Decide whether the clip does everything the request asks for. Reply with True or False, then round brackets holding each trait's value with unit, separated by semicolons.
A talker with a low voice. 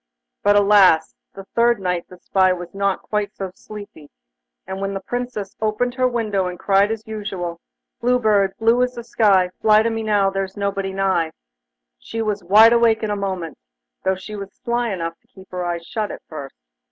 False (200 Hz)